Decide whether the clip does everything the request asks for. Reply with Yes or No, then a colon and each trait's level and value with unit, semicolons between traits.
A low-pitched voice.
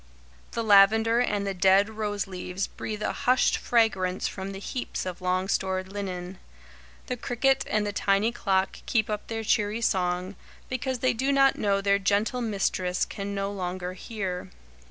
No: high, 200 Hz